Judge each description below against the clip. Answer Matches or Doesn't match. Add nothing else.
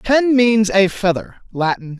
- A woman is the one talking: Doesn't match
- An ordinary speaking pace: Matches